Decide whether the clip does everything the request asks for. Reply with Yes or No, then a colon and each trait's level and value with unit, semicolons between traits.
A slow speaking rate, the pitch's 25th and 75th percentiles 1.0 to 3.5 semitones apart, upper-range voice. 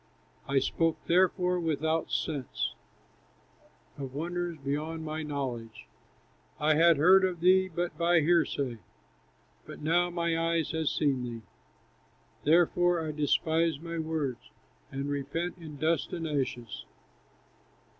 No: slow, 120 wpm; average, 3.1 semitones; medium, 160 Hz